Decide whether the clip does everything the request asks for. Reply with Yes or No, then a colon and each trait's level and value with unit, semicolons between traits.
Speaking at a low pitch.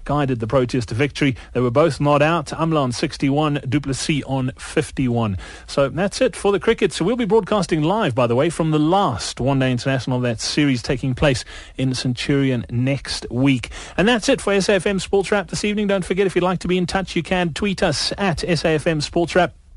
No: medium, 150 Hz